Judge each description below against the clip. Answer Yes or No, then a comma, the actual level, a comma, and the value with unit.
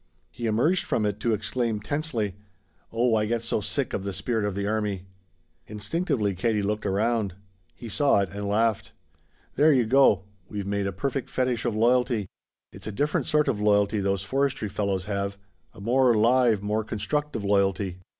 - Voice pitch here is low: Yes, low, 110 Hz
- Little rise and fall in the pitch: No, average, 3.4 semitones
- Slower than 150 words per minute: No, average, 175 wpm